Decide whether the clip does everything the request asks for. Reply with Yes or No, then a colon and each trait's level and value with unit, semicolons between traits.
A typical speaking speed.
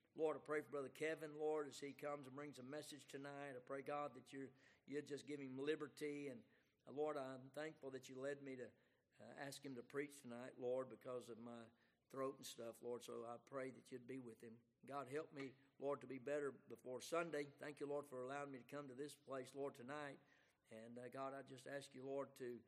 No: fast, 235 wpm